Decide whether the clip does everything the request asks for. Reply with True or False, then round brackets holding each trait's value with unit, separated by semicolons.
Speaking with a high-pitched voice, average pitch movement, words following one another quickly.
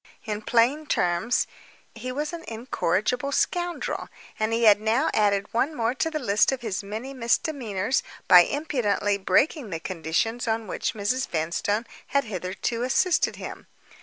False (230 Hz; 4.6 semitones; 150 wpm)